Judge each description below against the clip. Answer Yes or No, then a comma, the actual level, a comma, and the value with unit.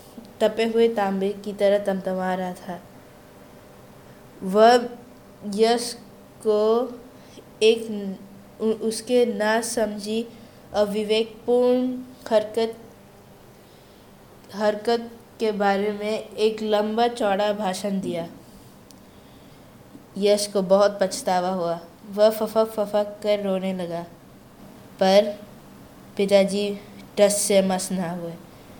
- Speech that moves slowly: Yes, slow, 90 wpm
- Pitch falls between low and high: No, high, 210 Hz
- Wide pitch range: No, narrow, 2.4 semitones